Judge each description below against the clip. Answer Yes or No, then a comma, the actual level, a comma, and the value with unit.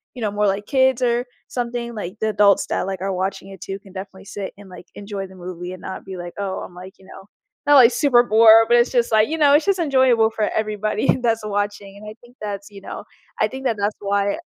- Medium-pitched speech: No, high, 210 Hz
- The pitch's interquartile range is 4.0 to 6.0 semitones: No, average, 3.5 semitones